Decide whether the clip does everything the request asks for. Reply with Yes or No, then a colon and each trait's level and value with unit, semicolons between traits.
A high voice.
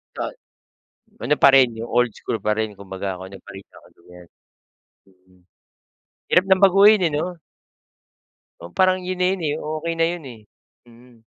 No: low, 125 Hz